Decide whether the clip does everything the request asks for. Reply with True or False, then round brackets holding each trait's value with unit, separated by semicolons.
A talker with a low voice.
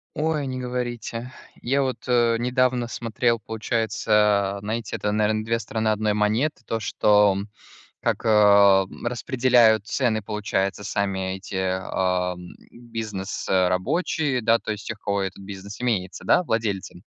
True (110 Hz)